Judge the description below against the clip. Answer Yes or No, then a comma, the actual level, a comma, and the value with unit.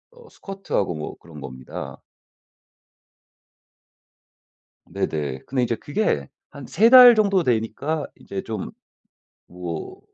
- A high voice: No, low, 120 Hz